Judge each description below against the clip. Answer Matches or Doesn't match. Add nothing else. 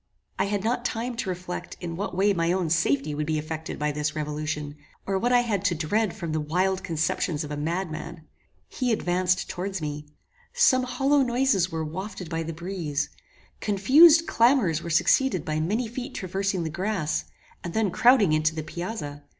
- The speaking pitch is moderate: Matches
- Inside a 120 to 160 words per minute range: Doesn't match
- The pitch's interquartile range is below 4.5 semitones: Doesn't match